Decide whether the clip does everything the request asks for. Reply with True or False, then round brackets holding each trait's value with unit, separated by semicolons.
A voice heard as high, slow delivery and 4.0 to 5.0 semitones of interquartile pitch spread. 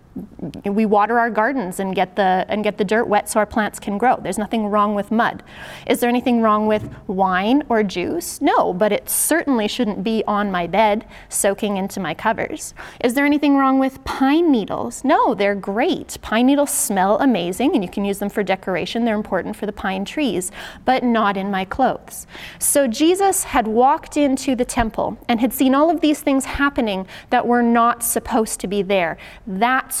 False (225 Hz; 195 wpm; 4.4 semitones)